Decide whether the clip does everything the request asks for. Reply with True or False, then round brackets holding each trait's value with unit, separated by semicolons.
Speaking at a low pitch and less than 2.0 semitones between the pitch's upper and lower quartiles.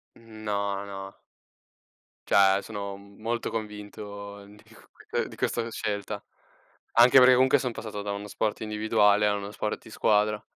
True (105 Hz; 1.3 semitones)